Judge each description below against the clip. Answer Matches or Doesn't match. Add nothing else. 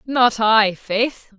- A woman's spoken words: Matches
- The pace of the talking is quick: Doesn't match